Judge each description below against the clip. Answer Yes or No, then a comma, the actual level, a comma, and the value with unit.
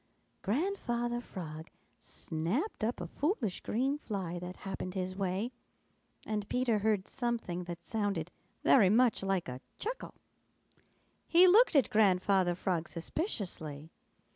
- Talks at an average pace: No, slow, 120 wpm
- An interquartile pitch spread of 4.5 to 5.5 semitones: Yes, average, 5.2 semitones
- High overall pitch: Yes, high, 200 Hz